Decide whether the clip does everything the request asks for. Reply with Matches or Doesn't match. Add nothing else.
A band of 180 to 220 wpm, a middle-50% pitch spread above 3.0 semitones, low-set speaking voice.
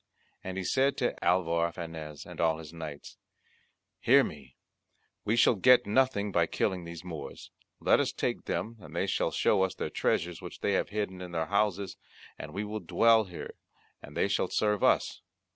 Matches